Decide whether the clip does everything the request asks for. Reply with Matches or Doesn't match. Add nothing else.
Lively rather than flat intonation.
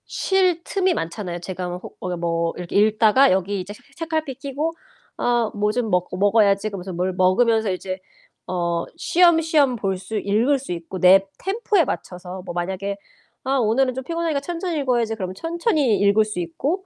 Matches